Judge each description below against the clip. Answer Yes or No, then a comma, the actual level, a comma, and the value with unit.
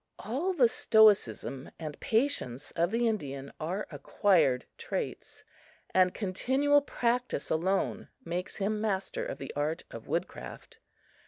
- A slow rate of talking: Yes, slow, 130 wpm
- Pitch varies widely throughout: Yes, wide, 7.2 semitones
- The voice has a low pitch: No, high, 195 Hz